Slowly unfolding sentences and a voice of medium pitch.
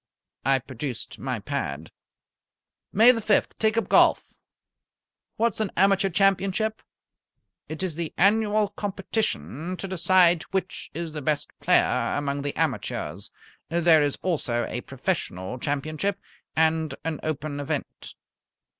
Yes: slow, 125 wpm; medium, 170 Hz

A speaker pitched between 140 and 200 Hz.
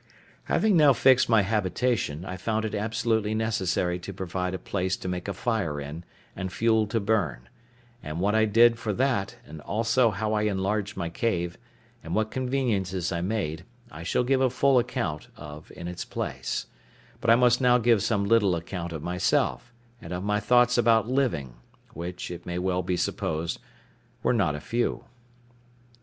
No: low, 105 Hz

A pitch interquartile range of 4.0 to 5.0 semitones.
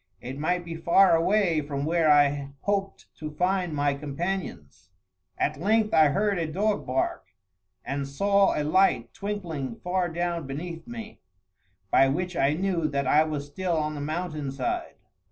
Yes: average, 4.7 semitones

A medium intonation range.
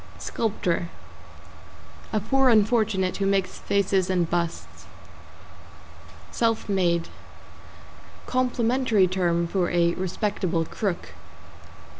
Yes: average, 4.0 semitones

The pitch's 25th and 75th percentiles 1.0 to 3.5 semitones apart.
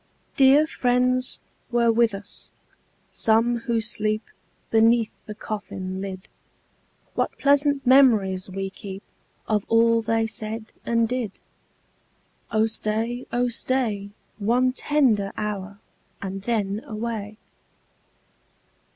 Yes: average, 2.8 semitones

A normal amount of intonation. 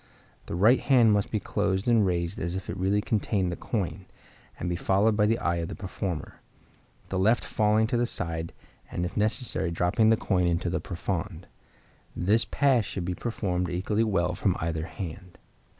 Yes: average, 3.5 semitones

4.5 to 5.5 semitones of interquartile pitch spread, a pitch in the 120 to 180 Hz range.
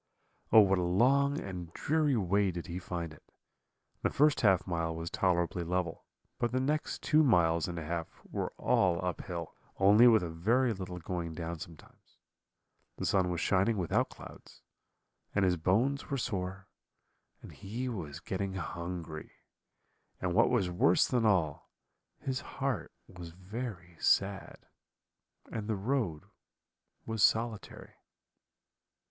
No: average, 4.8 semitones; very low, 95 Hz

